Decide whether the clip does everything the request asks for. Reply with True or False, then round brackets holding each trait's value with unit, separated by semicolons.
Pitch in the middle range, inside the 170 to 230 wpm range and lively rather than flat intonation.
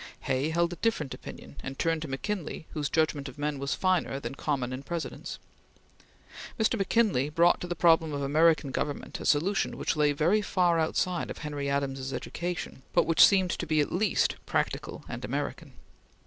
False (155 Hz; 180 wpm; 3.8 semitones)